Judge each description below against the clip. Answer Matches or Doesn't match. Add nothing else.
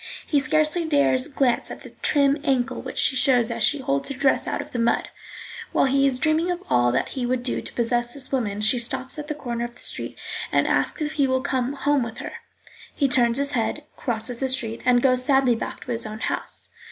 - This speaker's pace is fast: Matches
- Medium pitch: Doesn't match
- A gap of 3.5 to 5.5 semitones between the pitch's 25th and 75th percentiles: Doesn't match